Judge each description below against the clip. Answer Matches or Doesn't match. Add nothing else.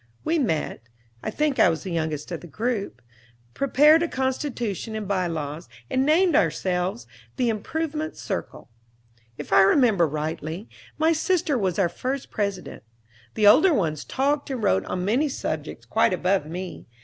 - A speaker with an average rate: Matches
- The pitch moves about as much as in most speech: Doesn't match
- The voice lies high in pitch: Matches